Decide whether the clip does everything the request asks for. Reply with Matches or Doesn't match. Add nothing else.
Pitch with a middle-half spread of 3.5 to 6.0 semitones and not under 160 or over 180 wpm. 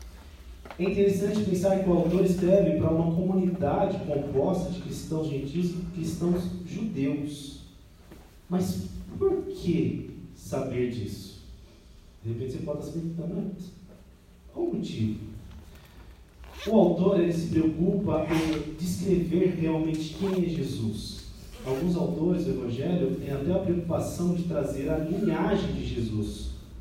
Doesn't match